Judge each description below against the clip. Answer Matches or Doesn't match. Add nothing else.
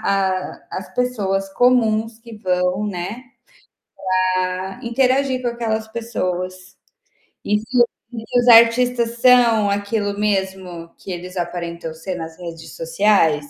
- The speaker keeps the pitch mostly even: Doesn't match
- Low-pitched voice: Doesn't match